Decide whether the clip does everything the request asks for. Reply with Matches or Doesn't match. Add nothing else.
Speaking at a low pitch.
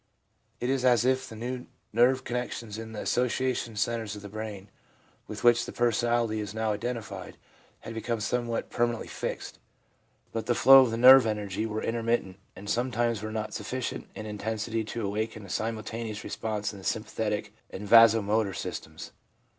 Matches